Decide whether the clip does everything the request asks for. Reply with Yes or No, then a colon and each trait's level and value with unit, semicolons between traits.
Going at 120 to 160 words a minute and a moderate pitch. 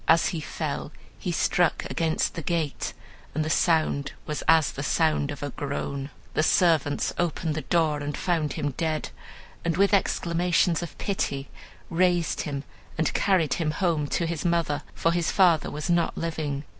No: average, 170 wpm; medium, 160 Hz